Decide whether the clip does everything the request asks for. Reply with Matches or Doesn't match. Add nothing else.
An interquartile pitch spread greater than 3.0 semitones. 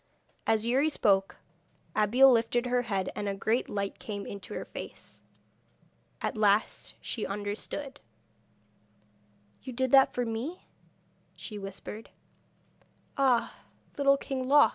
Matches